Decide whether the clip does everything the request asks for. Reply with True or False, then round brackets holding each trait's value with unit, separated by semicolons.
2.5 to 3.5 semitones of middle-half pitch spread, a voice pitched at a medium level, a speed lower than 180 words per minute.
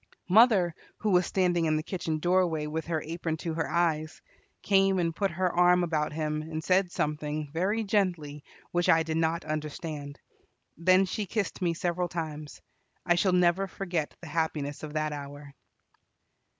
True (2.8 semitones; 165 Hz; 165 wpm)